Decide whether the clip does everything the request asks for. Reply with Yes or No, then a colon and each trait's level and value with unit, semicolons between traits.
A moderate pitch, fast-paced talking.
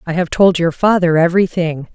No: medium, 170 Hz; average, 185 wpm